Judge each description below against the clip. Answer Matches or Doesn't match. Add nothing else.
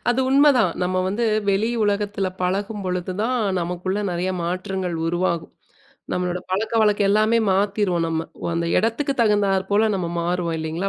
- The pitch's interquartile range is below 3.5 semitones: Matches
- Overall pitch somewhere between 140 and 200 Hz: Matches